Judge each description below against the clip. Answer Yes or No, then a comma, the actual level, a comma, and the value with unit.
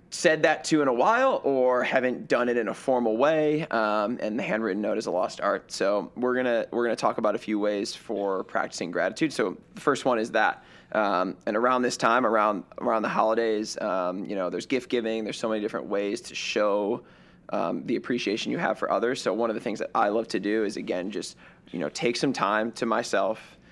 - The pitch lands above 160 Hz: No, low, 115 Hz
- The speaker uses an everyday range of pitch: Yes, average, 3.1 semitones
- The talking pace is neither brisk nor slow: No, fast, 235 wpm